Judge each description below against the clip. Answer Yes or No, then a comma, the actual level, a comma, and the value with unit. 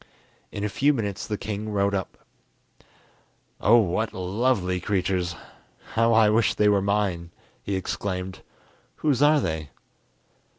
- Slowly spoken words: Yes, slow, 130 wpm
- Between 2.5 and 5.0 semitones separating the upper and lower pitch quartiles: Yes, average, 3.0 semitones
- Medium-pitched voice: No, low, 100 Hz